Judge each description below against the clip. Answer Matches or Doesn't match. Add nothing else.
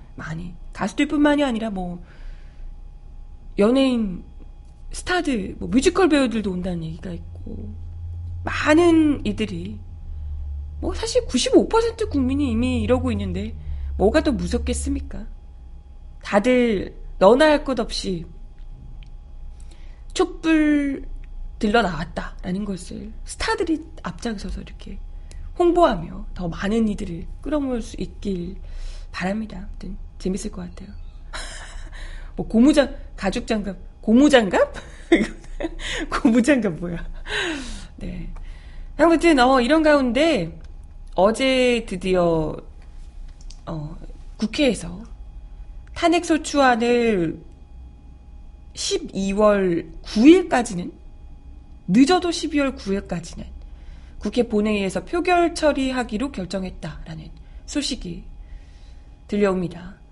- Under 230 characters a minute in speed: Matches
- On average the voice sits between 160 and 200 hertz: Matches